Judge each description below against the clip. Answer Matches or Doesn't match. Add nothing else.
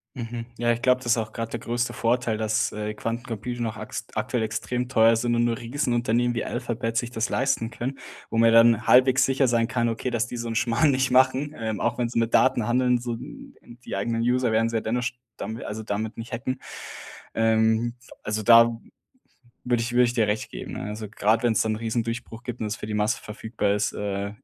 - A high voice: Doesn't match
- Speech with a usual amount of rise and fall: Doesn't match